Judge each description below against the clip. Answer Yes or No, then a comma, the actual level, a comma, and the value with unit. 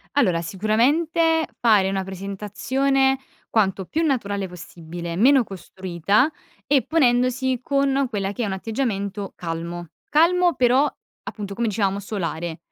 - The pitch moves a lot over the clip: Yes, wide, 5.9 semitones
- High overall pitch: Yes, high, 215 Hz